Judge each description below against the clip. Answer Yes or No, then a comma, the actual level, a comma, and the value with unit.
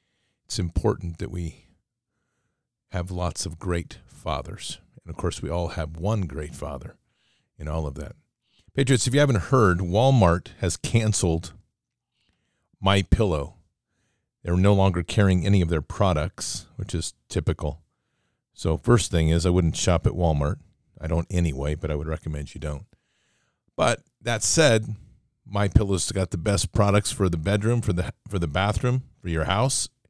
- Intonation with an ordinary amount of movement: Yes, average, 4.4 semitones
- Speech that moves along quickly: No, average, 160 wpm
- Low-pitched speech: Yes, very low, 95 Hz